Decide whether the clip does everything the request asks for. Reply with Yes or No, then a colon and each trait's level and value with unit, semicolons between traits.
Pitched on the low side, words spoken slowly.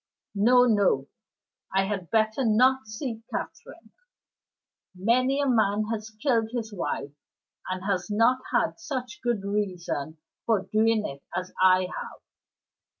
No: high, 215 Hz; slow, 130 wpm